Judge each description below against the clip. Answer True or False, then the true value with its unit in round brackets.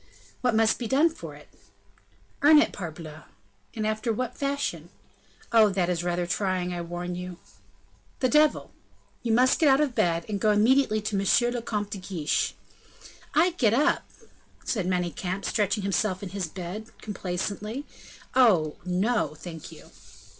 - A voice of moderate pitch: False (205 Hz)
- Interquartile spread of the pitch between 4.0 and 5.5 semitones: True (5.2 semitones)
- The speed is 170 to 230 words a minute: False (155 wpm)